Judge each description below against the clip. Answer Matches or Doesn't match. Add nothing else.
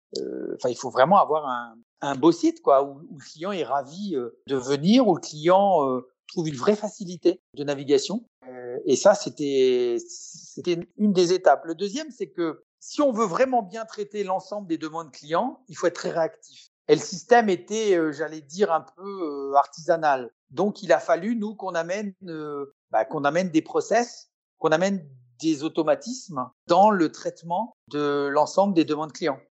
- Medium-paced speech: Matches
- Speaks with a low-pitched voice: Doesn't match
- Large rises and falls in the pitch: Matches